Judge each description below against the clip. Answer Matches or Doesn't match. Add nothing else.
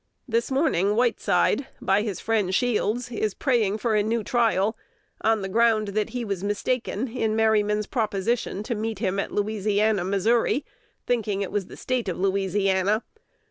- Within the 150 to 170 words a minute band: Matches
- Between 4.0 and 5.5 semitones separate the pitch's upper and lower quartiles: Doesn't match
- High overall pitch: Matches